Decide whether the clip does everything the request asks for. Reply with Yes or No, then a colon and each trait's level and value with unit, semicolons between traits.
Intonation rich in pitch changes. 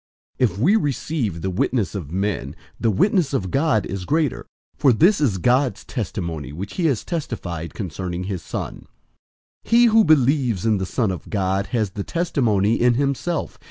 Yes: wide, 7.3 semitones